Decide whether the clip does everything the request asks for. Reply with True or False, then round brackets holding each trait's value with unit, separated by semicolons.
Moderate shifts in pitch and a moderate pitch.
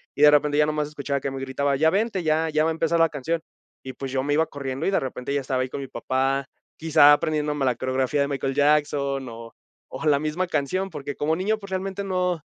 True (3.0 semitones; 145 Hz)